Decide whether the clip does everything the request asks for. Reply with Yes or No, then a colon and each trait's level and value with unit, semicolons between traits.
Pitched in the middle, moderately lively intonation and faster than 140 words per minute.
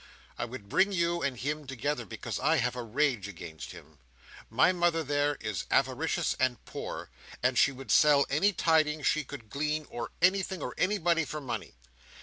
Yes: medium, 145 Hz; average, 4.9 semitones; average, 175 wpm